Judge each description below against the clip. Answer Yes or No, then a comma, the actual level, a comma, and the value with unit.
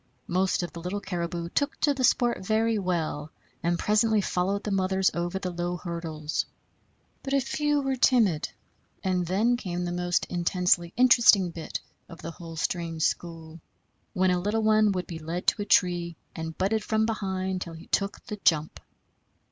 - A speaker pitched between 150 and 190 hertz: Yes, medium, 185 Hz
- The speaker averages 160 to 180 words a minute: Yes, average, 175 wpm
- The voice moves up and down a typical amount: Yes, average, 3.7 semitones